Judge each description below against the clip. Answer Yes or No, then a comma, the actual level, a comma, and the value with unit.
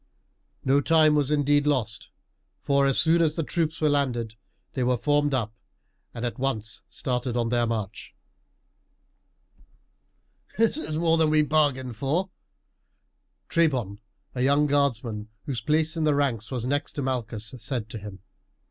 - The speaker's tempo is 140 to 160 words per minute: Yes, average, 150 wpm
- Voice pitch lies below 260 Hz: Yes, low, 135 Hz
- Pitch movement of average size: Yes, average, 4.2 semitones